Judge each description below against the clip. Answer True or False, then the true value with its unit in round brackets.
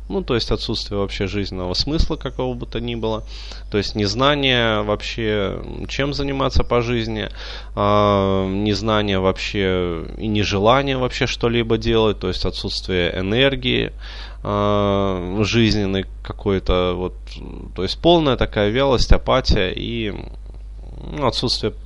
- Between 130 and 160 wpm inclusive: False (120 wpm)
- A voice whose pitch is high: False (105 Hz)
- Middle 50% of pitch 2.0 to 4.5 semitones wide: True (3.4 semitones)